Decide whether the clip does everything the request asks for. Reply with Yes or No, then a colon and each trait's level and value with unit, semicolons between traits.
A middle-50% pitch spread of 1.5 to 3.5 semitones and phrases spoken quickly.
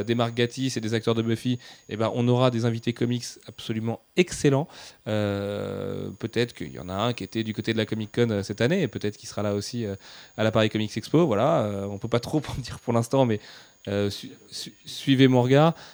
Yes: narrow, 2.6 semitones; fast, 230 wpm